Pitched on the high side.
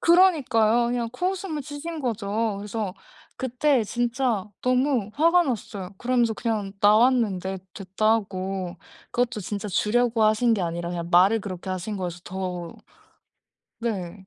Yes: high, 220 Hz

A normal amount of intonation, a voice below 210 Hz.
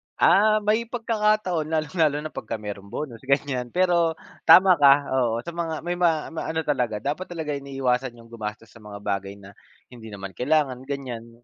No: wide, 6.2 semitones; medium, 140 Hz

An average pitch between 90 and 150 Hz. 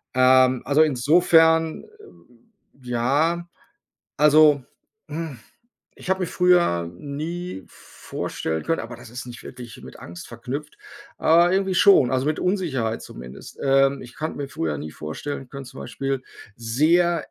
Yes: medium, 140 Hz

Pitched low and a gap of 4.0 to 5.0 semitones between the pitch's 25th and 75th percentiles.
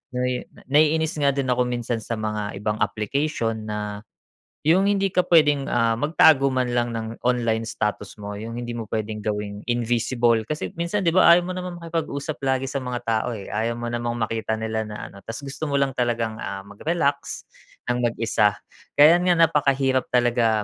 Yes: low, 120 Hz; average, 4.4 semitones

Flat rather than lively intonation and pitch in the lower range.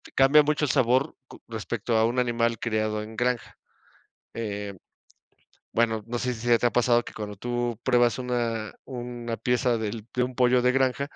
Yes: narrow, 1.8 semitones; low, 120 Hz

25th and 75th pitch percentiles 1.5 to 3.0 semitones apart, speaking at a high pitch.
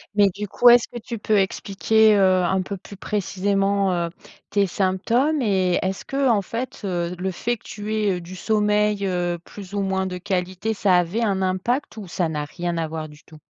Yes: narrow, 2.6 semitones; high, 195 Hz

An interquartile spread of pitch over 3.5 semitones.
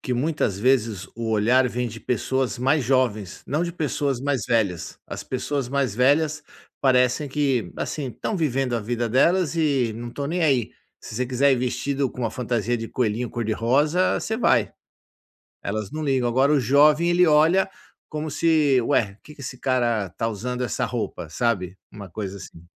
Yes: average, 4.0 semitones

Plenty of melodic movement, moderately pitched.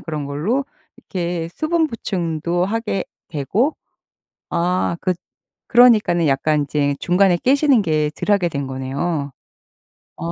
Yes: wide, 5.7 semitones; medium, 175 Hz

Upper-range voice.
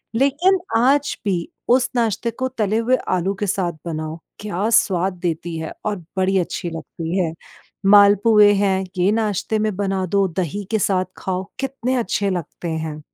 Yes: high, 200 Hz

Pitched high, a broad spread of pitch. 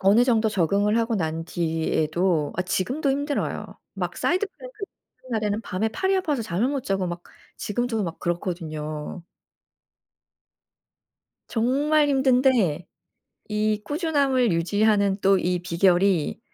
Yes: high, 210 Hz; wide, 6.7 semitones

